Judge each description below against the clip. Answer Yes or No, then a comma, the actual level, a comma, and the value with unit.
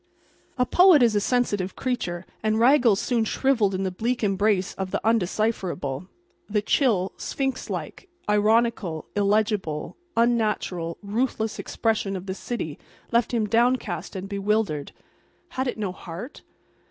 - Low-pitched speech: No, high, 215 Hz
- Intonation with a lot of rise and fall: No, average, 3.8 semitones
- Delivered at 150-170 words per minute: No, slow, 135 wpm